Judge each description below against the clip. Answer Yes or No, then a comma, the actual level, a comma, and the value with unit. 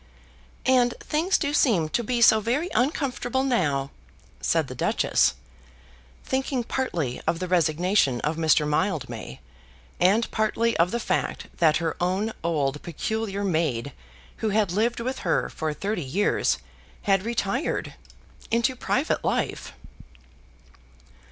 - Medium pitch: No, high, 200 Hz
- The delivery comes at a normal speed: No, slow, 125 wpm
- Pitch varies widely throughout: Yes, wide, 6.8 semitones